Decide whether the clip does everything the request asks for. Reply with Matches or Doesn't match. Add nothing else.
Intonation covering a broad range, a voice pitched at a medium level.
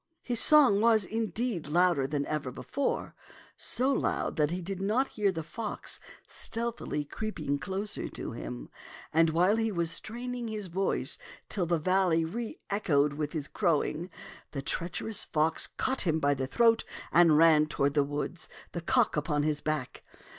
Matches